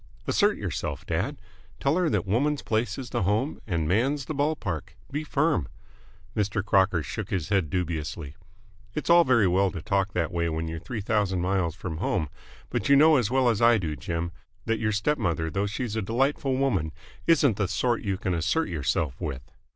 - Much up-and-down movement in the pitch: Yes, wide, 7.1 semitones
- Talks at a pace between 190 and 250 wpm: Yes, average, 195 wpm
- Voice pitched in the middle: No, low, 100 Hz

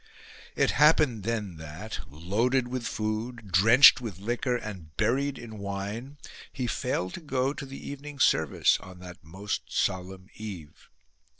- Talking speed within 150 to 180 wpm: No, average, 140 wpm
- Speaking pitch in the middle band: No, low, 110 Hz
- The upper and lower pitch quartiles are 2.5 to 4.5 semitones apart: No, wide, 5.4 semitones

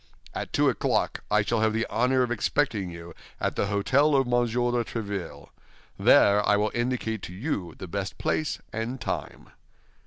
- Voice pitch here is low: Yes, low, 110 Hz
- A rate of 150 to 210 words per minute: Yes, average, 175 wpm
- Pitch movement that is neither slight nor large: Yes, average, 3.4 semitones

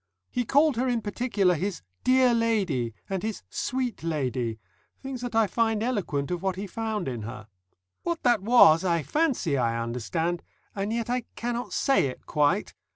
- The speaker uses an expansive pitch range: Yes, wide, 7.6 semitones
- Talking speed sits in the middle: Yes, average, 170 wpm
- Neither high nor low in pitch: No, high, 205 Hz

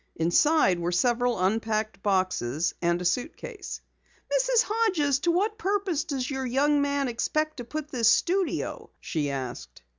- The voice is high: Yes, very high, 255 Hz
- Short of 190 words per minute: Yes, average, 145 wpm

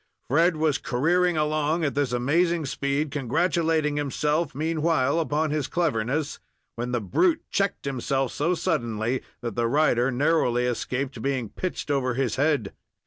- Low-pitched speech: No, medium, 145 Hz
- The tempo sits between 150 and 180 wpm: No, average, 140 wpm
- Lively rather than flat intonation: No, average, 4.3 semitones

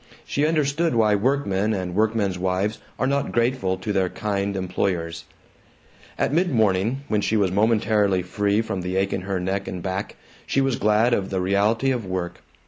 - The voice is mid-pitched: No, low, 100 Hz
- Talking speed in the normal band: Yes, average, 180 wpm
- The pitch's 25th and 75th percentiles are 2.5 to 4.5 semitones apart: Yes, average, 3.4 semitones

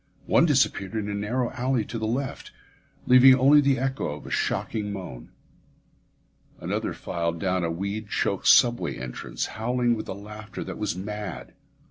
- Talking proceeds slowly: No, average, 160 wpm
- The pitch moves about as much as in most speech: Yes, average, 4.6 semitones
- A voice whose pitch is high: No, low, 105 Hz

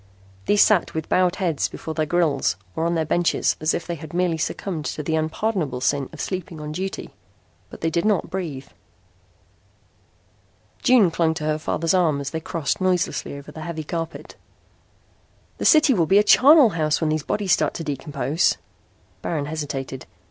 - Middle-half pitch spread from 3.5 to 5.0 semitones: No, average, 2.9 semitones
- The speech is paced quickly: No, average, 175 wpm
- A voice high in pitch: No, medium, 160 Hz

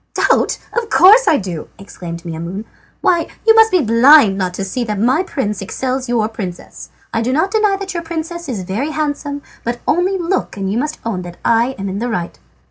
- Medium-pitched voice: No, high, 245 Hz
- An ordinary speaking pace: No, fast, 215 wpm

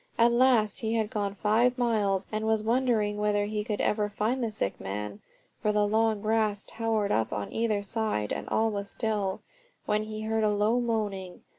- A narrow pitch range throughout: Yes, narrow, 1.6 semitones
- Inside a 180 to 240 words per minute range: Yes, average, 190 wpm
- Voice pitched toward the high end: Yes, high, 215 Hz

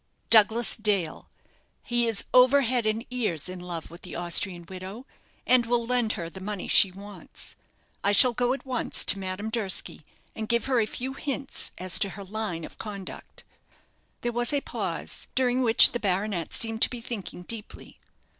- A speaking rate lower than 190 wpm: Yes, average, 180 wpm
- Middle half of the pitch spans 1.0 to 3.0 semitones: No, average, 4.3 semitones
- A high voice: Yes, high, 220 Hz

